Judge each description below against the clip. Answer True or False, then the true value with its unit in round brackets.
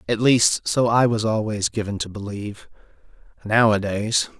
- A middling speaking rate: False (125 wpm)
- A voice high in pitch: False (110 Hz)